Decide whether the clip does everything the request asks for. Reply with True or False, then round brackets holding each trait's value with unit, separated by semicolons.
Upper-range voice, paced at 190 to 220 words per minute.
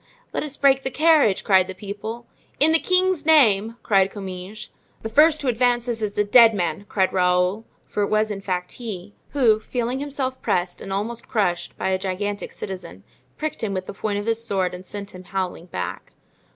True (210 Hz; 195 wpm)